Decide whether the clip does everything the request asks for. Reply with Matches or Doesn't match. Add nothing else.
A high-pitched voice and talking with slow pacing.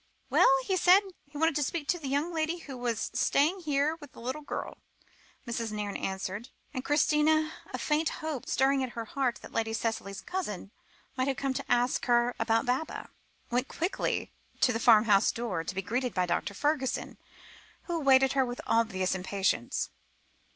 Doesn't match